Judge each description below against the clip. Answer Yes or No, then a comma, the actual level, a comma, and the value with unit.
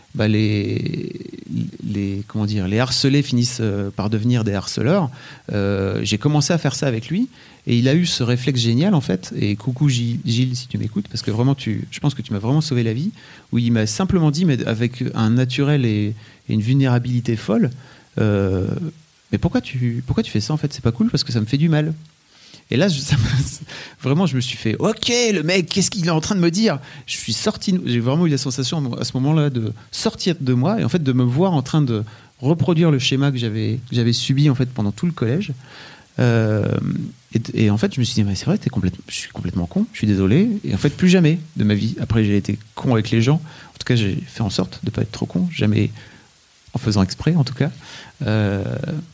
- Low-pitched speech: Yes, low, 130 Hz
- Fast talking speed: Yes, fast, 240 wpm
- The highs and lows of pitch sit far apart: Yes, wide, 5.7 semitones